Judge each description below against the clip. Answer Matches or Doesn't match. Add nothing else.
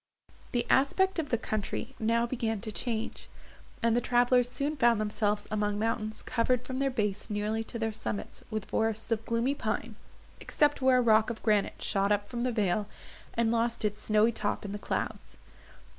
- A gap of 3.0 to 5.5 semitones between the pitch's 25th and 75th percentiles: Doesn't match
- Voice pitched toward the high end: Matches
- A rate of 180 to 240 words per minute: Matches